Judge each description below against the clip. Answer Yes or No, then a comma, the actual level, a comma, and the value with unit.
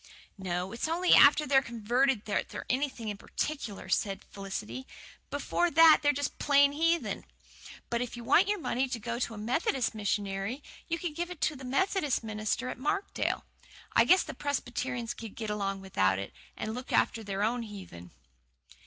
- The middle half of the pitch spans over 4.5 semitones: Yes, wide, 5.6 semitones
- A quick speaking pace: No, average, 180 wpm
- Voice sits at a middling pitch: No, high, 245 Hz